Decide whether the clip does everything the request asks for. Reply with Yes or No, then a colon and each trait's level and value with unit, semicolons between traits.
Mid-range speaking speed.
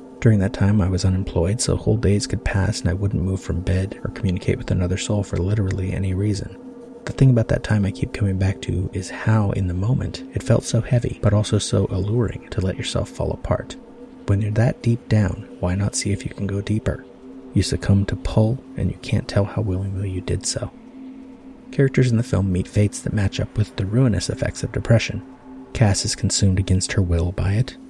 No: fast, 220 wpm